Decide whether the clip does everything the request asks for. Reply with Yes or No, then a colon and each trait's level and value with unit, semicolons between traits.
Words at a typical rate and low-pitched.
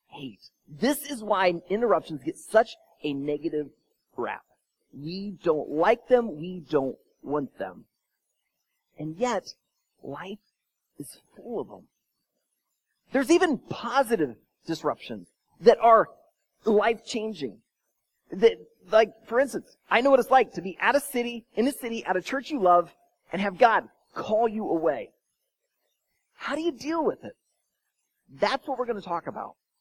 No: average, 145 wpm; high, 225 Hz